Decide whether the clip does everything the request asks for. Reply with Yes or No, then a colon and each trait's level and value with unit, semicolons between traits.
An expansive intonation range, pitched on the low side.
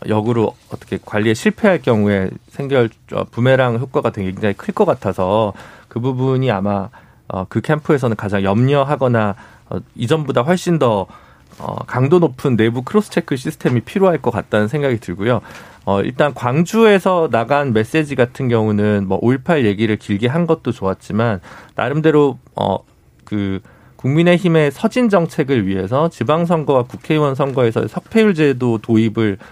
Yes: wide, 6.1 semitones; low, 125 Hz